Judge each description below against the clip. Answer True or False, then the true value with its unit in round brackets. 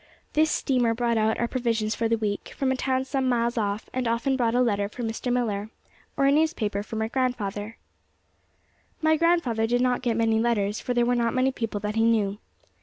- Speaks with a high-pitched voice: True (235 Hz)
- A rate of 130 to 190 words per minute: False (205 wpm)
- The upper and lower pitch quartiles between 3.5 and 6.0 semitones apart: False (2.6 semitones)